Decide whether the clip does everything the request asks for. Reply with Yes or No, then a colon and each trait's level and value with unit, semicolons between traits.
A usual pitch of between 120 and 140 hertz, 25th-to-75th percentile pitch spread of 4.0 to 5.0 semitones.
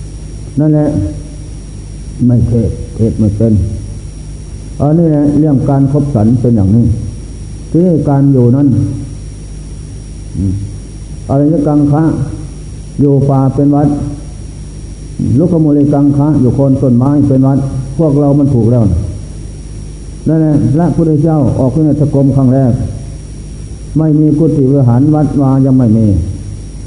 Yes: low, 135 Hz; average, 4.3 semitones